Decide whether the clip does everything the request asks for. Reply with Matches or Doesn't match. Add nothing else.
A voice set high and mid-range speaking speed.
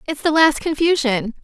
Matches